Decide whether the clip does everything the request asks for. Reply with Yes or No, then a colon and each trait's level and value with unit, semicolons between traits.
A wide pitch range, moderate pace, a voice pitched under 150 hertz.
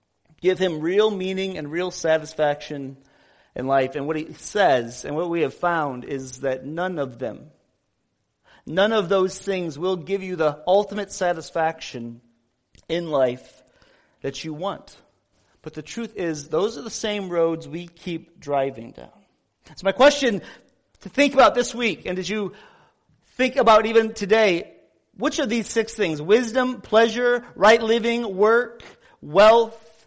No: wide, 6.1 semitones; average, 155 wpm; medium, 185 Hz